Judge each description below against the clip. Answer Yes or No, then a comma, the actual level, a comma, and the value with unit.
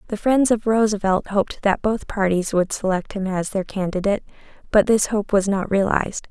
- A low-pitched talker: No, high, 200 Hz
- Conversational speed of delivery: Yes, average, 190 wpm